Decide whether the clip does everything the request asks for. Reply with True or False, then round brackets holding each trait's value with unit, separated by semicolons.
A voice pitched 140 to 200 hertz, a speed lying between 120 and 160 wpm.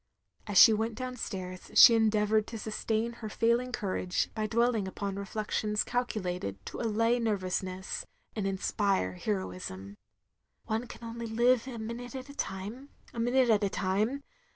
False (220 Hz; 155 wpm)